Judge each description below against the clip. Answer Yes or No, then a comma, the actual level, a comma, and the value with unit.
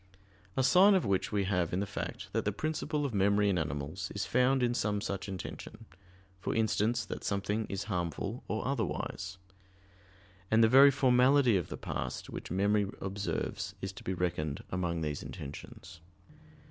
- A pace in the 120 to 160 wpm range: No, average, 170 wpm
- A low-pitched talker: Yes, low, 100 Hz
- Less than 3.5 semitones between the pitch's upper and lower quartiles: No, average, 4.6 semitones